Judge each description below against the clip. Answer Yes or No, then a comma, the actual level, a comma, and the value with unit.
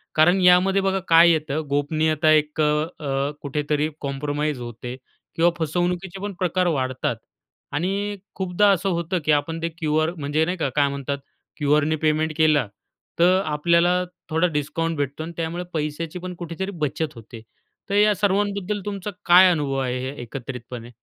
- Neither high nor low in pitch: Yes, medium, 160 Hz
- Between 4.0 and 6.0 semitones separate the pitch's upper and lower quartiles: No, average, 3.6 semitones